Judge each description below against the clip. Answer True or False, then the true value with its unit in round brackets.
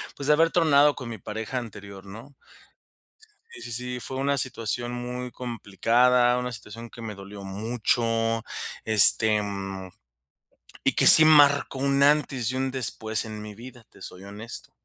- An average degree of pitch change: True (3.5 semitones)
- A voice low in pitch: True (120 Hz)